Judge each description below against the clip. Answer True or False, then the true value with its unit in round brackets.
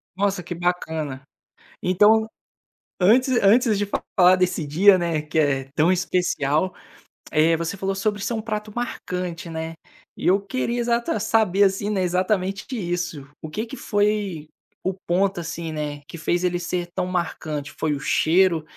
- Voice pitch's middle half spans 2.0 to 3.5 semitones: False (4.0 semitones)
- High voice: False (180 Hz)